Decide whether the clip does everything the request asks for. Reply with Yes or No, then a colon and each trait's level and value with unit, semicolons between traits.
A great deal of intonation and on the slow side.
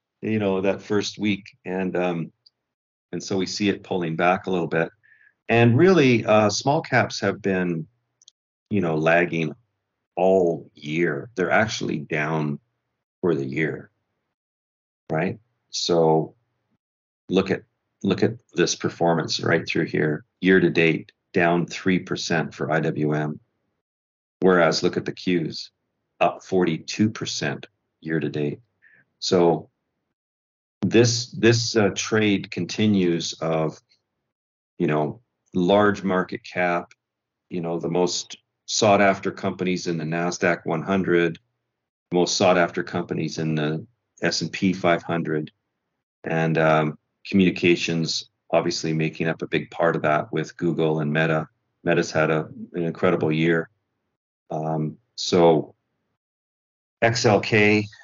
No: average, 3.4 semitones; slow, 120 wpm